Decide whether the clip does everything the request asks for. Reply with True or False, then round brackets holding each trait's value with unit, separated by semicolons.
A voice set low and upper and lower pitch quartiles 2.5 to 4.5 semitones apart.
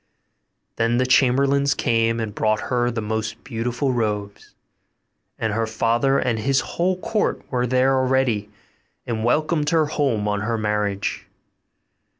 True (120 Hz; 3.5 semitones)